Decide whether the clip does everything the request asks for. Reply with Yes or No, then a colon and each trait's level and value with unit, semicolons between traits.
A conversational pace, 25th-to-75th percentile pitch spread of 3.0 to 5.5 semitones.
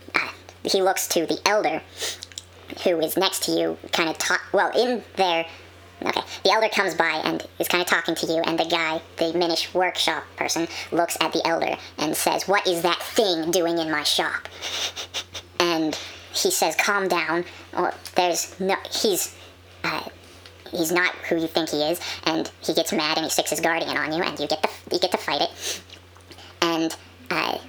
Yes: average, 195 wpm; average, 3.4 semitones